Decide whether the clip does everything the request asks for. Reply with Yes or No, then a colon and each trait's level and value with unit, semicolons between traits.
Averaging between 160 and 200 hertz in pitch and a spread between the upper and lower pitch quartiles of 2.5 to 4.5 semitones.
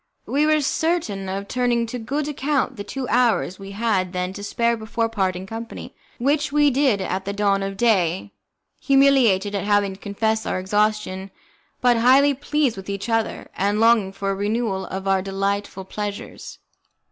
No: high, 210 Hz; average, 4.1 semitones